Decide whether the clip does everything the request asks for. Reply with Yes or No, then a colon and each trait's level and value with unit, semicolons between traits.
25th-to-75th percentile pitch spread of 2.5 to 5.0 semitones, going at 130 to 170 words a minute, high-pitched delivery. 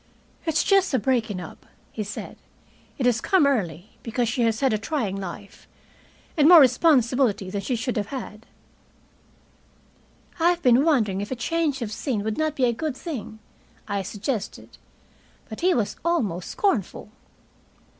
No: wide, 5.5 semitones; average, 160 wpm; high, 240 Hz